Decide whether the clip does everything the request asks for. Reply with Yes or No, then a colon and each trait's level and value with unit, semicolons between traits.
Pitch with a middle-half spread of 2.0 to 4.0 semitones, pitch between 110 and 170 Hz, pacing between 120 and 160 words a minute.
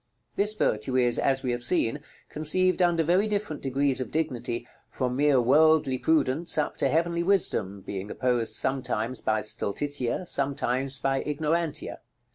No: average, 4.5 semitones; low, 135 Hz; average, 145 wpm